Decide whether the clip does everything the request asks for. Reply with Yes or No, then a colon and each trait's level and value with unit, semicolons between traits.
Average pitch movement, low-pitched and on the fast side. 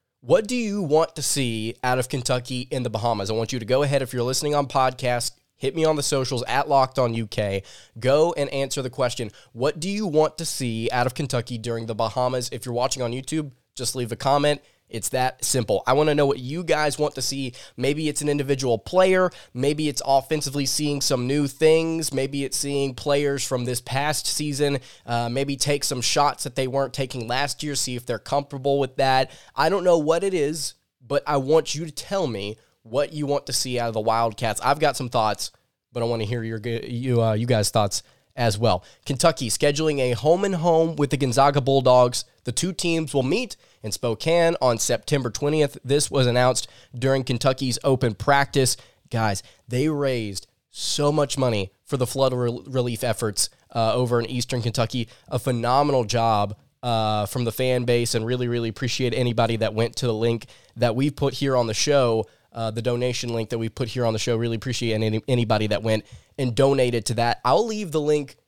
Yes: average, 3.3 semitones; low, 130 Hz; fast, 210 wpm